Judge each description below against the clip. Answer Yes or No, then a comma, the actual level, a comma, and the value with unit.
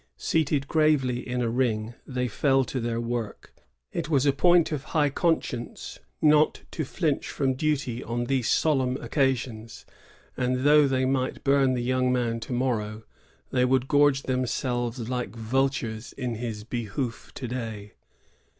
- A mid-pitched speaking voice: No, low, 130 Hz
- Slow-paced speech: No, average, 155 wpm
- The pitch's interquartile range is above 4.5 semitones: No, narrow, 2.6 semitones